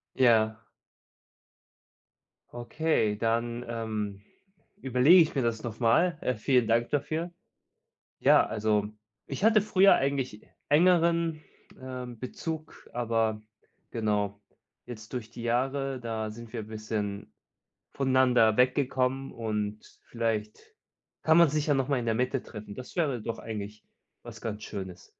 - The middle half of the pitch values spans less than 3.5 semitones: No, average, 3.8 semitones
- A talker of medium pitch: No, low, 120 Hz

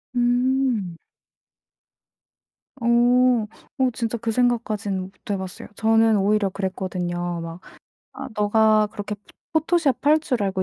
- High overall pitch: Yes, high, 215 Hz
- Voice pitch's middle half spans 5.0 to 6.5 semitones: No, average, 4.3 semitones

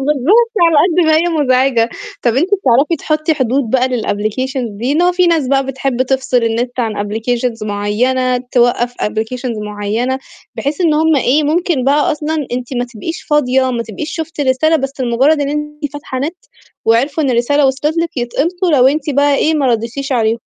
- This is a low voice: No, very high, 265 Hz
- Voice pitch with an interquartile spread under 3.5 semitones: No, average, 3.8 semitones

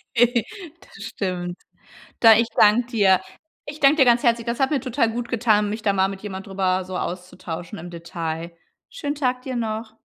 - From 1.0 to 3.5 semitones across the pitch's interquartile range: No, average, 4.6 semitones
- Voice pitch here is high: Yes, high, 220 Hz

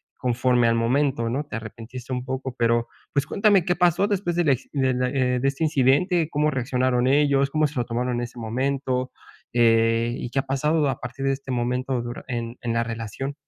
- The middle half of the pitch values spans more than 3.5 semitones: No, average, 2.8 semitones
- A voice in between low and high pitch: No, low, 130 Hz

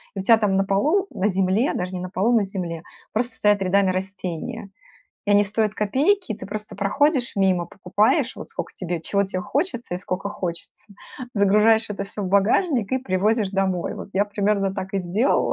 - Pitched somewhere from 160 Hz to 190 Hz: No, high, 200 Hz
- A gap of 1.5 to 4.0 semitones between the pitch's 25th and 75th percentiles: Yes, narrow, 2.6 semitones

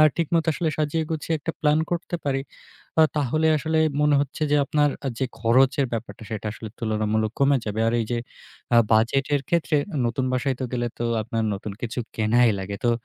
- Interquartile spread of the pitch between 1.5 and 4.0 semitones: No, average, 4.8 semitones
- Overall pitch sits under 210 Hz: Yes, low, 135 Hz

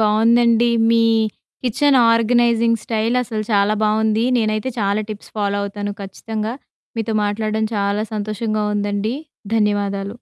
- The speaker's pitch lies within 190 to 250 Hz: Yes, high, 215 Hz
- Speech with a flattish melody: Yes, narrow, 1.9 semitones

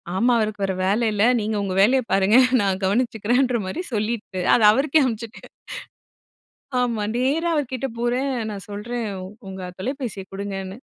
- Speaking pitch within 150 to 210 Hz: No, high, 220 Hz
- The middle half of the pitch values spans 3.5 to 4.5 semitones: Yes, average, 4.0 semitones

